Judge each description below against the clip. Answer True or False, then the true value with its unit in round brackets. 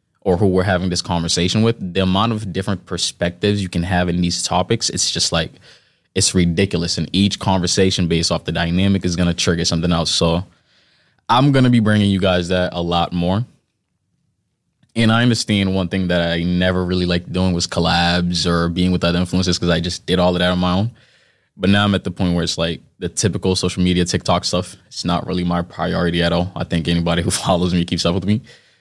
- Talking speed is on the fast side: True (220 wpm)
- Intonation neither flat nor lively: False (1.8 semitones)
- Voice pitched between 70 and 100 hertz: True (90 Hz)